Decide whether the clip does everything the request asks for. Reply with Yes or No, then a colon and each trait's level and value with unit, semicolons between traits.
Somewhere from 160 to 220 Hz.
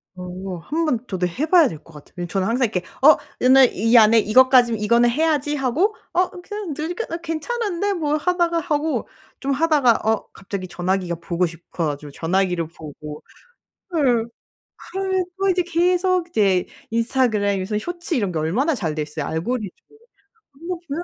No: high, 240 Hz